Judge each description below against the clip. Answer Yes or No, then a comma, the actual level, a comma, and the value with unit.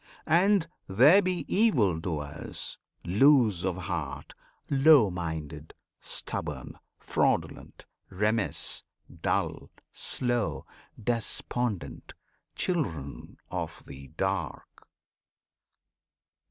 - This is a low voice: Yes, low, 105 Hz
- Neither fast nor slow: No, slow, 75 wpm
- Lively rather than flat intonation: Yes, wide, 8.4 semitones